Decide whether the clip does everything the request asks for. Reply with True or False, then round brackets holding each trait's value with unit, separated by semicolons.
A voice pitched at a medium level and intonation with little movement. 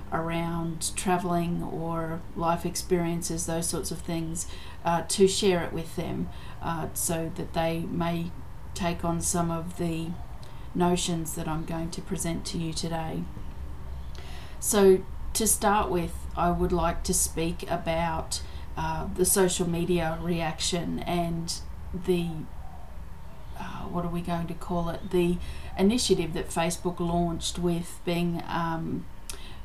True (170 Hz; 1.2 semitones)